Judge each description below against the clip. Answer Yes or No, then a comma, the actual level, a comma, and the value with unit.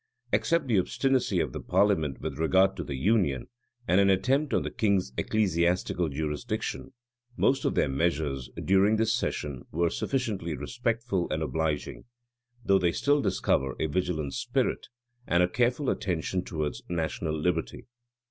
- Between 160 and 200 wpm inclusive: No, average, 150 wpm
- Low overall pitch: Yes, very low, 90 Hz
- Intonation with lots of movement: Yes, wide, 5.7 semitones